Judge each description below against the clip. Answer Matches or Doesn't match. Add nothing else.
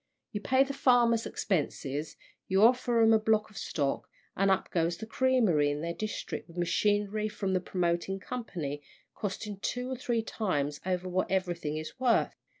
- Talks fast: Doesn't match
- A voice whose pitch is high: Matches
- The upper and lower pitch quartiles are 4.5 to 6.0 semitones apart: Matches